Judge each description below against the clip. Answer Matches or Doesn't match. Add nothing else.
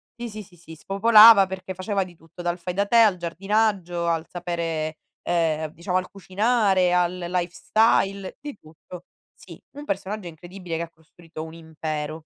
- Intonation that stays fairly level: Doesn't match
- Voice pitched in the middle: Matches